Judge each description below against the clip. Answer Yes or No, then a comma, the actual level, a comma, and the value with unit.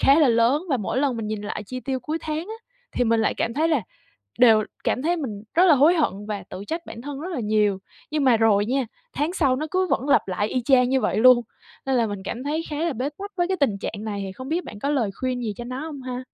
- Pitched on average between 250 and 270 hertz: Yes, very high, 255 Hz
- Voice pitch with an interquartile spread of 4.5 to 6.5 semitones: Yes, average, 5.1 semitones